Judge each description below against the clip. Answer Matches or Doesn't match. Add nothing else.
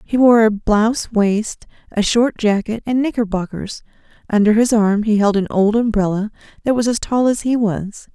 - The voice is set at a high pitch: Matches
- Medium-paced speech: Matches